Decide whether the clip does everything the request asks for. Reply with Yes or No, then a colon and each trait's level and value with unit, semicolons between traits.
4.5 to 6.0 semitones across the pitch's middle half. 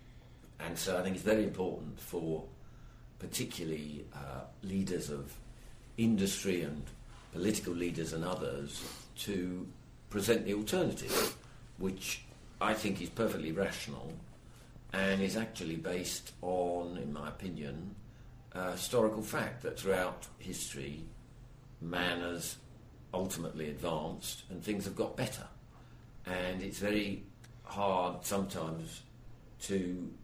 No: average, 4.0 semitones